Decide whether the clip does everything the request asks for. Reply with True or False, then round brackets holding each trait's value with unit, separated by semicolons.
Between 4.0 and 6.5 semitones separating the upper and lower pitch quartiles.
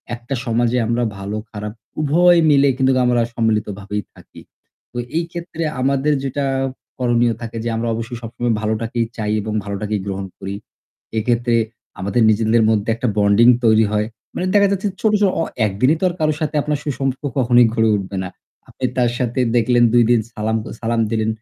False (3.4 semitones)